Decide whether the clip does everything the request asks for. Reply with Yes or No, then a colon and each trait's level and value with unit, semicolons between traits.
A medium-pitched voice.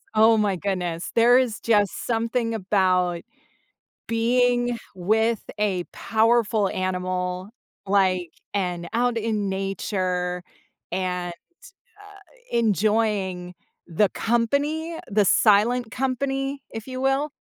No: high, 215 Hz